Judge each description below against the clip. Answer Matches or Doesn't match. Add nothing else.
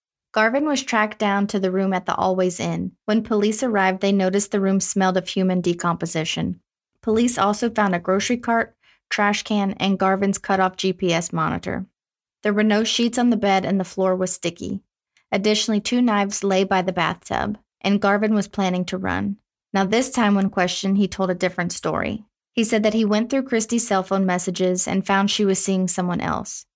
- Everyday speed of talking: Matches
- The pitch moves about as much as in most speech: Doesn't match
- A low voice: Doesn't match